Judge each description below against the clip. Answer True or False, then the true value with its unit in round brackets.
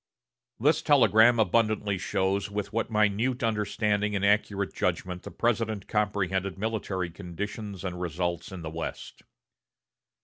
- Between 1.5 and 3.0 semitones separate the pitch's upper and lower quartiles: True (2.7 semitones)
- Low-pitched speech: True (105 Hz)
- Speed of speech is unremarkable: False (125 wpm)